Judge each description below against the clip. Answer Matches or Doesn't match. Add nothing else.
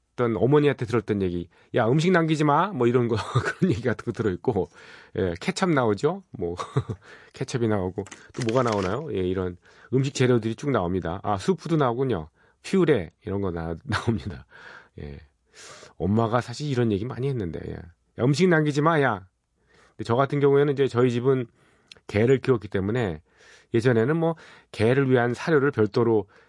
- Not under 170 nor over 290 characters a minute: Doesn't match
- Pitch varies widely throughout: Matches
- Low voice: Matches